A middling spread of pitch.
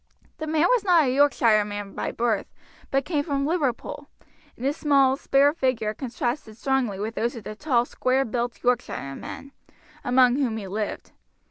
Yes: average, 3.9 semitones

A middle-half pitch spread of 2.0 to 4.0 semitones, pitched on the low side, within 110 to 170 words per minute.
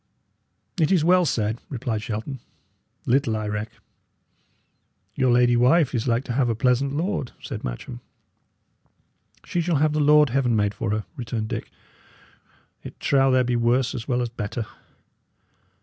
Yes: average, 3.7 semitones; low, 125 Hz; average, 155 wpm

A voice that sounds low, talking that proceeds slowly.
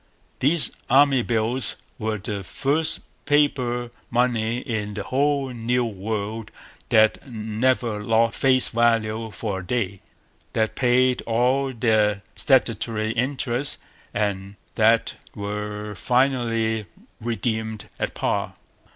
Yes: low, 115 Hz; slow, 110 wpm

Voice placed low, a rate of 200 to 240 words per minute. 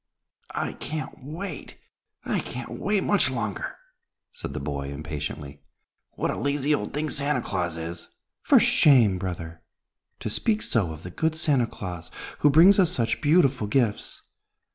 No: low, 120 Hz; average, 150 wpm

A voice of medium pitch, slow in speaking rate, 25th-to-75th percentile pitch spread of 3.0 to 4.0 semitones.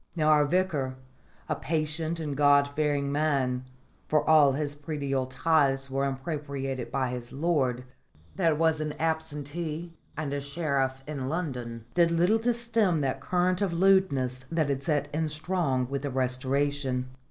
No: medium, 145 Hz; average, 155 wpm; average, 3.3 semitones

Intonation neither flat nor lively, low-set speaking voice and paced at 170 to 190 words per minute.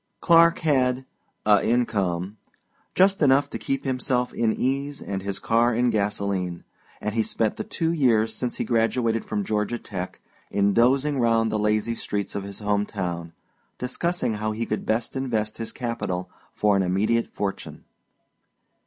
No: average, 3.7 semitones; low, 115 Hz; average, 160 wpm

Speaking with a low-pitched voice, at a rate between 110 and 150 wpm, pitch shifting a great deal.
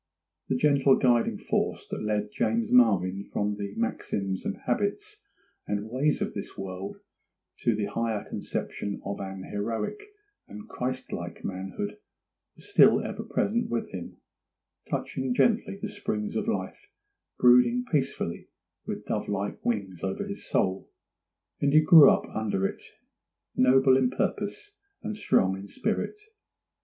Yes: low, 115 Hz; average, 140 wpm; wide, 6.9 semitones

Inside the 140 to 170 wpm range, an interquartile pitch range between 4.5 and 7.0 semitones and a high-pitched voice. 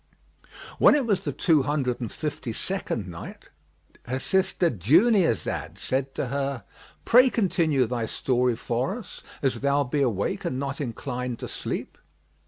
No: average, 150 wpm; average, 4.8 semitones; low, 135 Hz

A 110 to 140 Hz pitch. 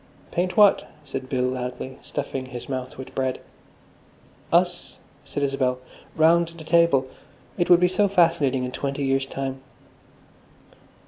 Yes: low, 135 Hz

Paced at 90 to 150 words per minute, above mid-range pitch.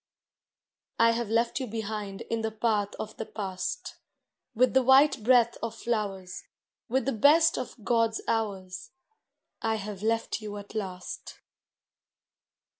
Yes: slow, 135 wpm; high, 220 Hz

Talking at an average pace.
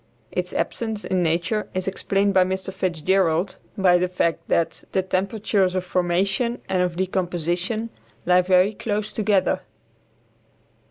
No: slow, 130 wpm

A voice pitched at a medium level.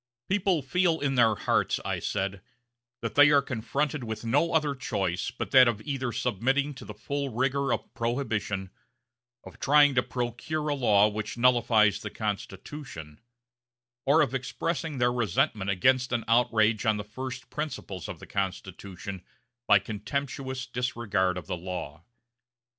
No: low, 120 Hz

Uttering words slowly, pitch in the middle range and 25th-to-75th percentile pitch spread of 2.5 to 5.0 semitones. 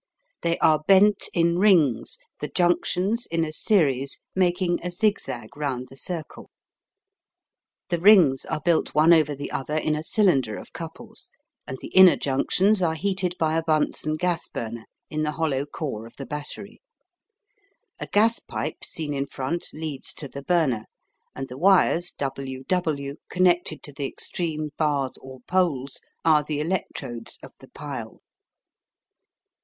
No: average, 150 wpm; medium, 155 Hz; average, 4.3 semitones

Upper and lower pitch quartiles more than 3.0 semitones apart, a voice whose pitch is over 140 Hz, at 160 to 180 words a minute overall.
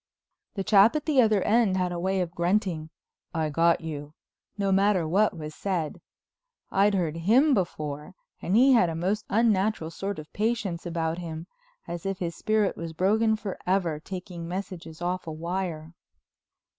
Yes: average, 3.6 semitones; medium, 185 Hz; average, 165 wpm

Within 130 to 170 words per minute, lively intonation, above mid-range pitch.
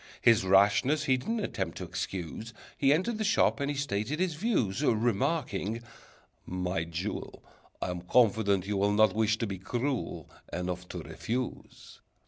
No: average, 150 wpm; wide, 6.6 semitones; low, 110 Hz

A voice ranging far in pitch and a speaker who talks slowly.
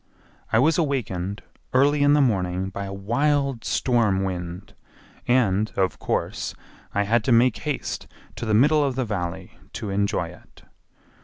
No: wide, 5.7 semitones; average, 155 wpm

